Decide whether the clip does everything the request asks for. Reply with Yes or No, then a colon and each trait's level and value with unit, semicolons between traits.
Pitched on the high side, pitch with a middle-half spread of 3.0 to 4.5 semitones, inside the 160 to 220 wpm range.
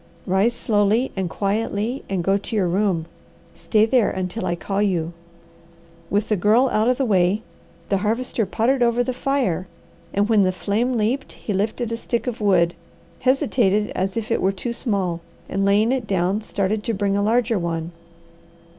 Yes: high, 210 Hz; average, 3.3 semitones; average, 180 wpm